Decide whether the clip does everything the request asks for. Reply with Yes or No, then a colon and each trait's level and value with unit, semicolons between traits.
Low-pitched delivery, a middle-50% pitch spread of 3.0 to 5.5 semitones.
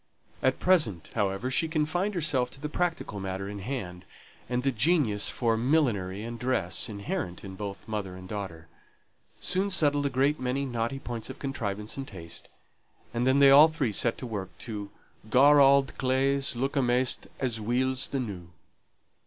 Yes: low, 125 Hz; average, 5.2 semitones